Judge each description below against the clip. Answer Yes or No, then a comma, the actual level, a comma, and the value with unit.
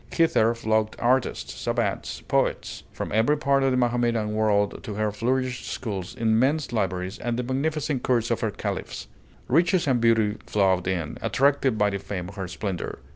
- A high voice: No, low, 115 Hz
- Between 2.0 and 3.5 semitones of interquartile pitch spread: No, average, 3.9 semitones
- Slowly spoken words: No, average, 170 wpm